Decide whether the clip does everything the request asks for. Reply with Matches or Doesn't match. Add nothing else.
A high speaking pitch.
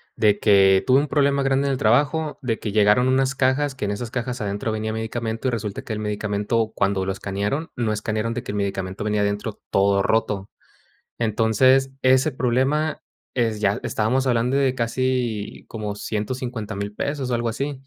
Doesn't match